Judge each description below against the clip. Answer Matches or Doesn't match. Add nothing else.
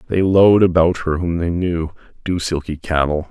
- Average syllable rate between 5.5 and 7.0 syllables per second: Doesn't match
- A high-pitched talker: Doesn't match